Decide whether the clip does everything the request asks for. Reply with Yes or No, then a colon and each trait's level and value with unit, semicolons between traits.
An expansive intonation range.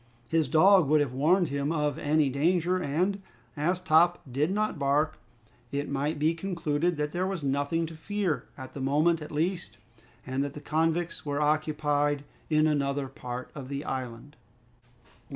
No: average, 2.9 semitones